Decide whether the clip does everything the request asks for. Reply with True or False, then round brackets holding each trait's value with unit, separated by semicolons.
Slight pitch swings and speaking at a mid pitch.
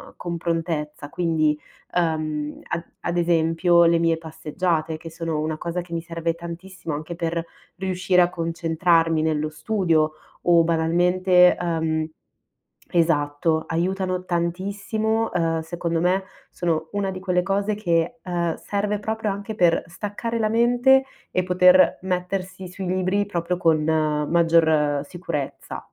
True (2.3 semitones; 170 Hz)